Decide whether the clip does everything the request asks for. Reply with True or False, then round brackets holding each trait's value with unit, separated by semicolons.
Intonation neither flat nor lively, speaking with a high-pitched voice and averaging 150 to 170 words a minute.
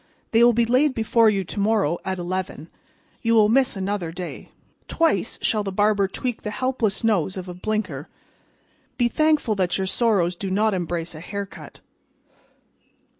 True (3.6 semitones; 205 Hz; 165 wpm)